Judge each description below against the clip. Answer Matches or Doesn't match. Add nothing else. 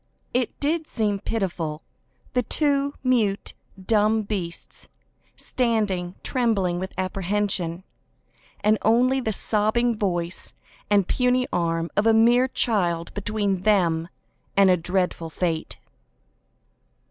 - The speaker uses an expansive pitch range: Doesn't match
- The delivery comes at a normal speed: Doesn't match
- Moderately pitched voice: Doesn't match